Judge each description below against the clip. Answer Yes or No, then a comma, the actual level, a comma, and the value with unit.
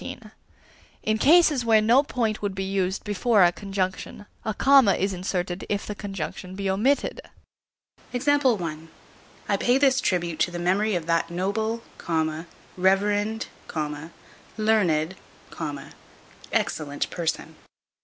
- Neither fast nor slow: No, slow, 115 wpm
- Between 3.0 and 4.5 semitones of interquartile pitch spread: Yes, average, 3.6 semitones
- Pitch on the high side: Yes, high, 200 Hz